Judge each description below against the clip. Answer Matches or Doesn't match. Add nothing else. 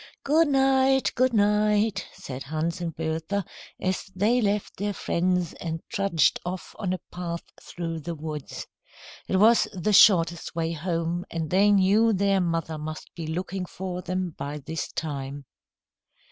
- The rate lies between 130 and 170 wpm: Matches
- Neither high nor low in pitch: Matches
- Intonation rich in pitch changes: Doesn't match